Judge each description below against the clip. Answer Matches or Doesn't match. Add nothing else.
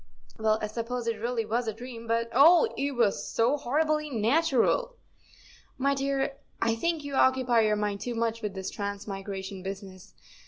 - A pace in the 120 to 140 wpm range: Doesn't match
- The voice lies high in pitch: Matches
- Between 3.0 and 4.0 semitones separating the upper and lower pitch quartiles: Doesn't match